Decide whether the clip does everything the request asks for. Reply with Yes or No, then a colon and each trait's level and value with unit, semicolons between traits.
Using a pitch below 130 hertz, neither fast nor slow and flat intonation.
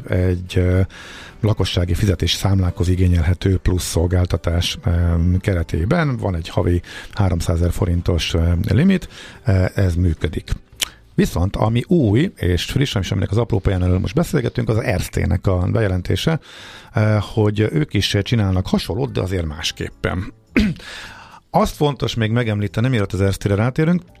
No: very low, 95 Hz; average, 125 wpm; average, 3.8 semitones